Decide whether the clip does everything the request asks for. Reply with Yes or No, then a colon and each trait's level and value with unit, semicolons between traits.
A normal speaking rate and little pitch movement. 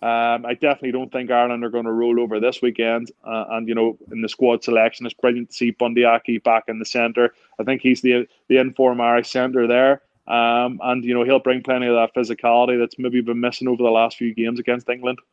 No: fast, 230 wpm; narrow, 1.2 semitones